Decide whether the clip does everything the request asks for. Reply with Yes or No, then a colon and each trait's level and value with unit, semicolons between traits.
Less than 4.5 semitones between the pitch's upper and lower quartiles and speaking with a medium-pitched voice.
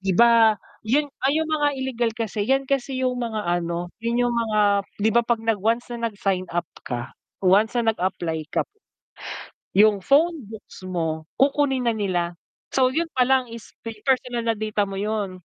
No: average, 4.1 semitones; high, 225 Hz